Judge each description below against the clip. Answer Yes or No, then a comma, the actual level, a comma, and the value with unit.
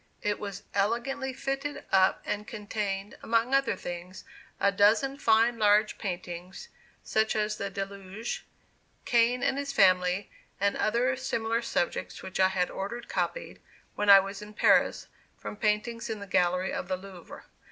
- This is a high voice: Yes, high, 210 Hz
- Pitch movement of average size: Yes, average, 3.2 semitones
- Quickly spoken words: No, average, 150 wpm